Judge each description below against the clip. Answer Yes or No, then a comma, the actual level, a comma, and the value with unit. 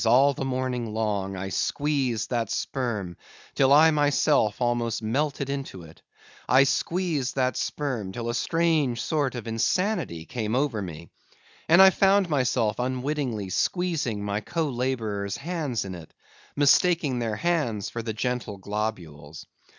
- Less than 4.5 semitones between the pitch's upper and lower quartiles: No, average, 5.2 semitones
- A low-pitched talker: Yes, low, 125 Hz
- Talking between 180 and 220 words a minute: No, average, 145 wpm